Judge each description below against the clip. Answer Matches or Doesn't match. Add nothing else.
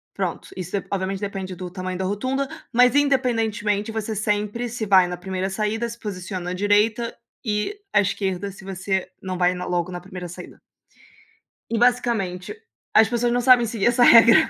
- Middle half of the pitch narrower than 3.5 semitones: Doesn't match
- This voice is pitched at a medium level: Doesn't match